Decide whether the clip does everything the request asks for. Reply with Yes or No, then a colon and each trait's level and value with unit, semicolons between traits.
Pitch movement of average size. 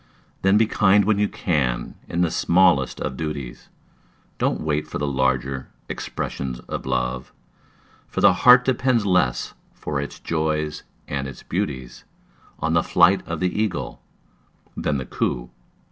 No: wide, 6.1 semitones